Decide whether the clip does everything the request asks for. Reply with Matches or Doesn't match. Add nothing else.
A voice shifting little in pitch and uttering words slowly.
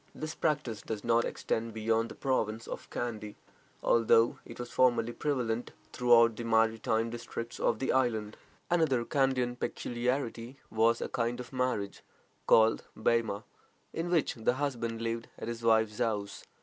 Doesn't match